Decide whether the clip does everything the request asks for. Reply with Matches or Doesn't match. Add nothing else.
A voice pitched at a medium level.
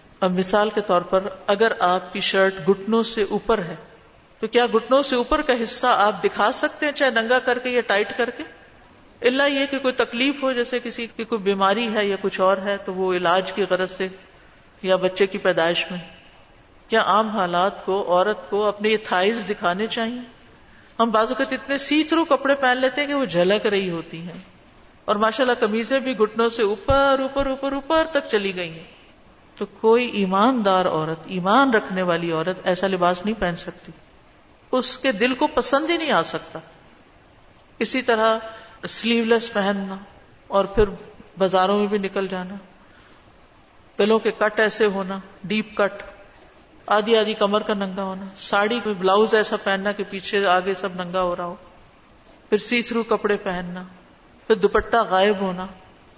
Doesn't match